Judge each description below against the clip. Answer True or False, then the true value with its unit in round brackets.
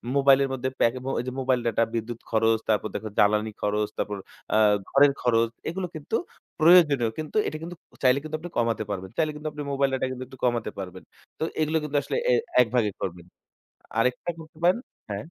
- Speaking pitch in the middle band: False (130 Hz)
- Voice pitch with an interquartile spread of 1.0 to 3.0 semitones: False (5.3 semitones)